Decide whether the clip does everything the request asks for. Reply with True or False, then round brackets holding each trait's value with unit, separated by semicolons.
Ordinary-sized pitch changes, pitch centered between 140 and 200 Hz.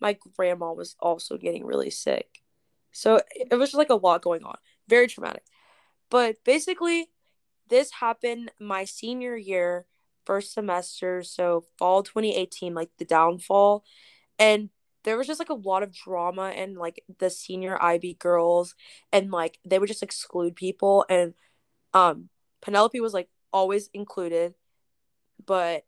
True (4.0 semitones; 190 Hz)